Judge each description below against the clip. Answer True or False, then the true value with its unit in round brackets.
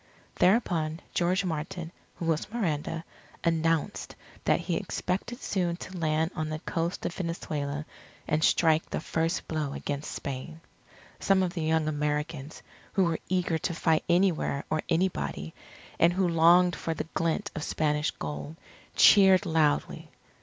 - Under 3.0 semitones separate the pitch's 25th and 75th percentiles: True (2.5 semitones)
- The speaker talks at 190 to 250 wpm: False (145 wpm)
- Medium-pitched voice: True (165 Hz)